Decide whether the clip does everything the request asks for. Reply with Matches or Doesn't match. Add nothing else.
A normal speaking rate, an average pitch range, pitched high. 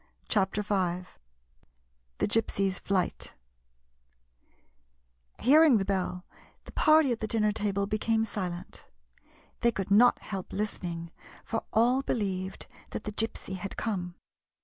Doesn't match